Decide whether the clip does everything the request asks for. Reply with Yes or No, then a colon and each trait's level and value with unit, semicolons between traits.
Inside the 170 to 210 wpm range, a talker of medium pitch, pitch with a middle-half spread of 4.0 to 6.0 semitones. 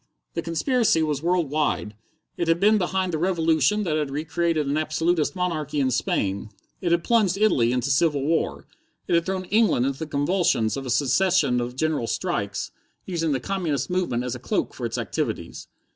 Yes: average, 185 wpm; medium, 160 Hz; average, 4.6 semitones